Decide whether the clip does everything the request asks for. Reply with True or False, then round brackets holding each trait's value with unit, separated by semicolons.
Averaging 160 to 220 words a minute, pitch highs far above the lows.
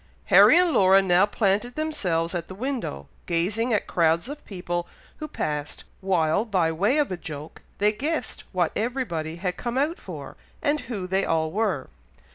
True (170 wpm; 6.3 semitones)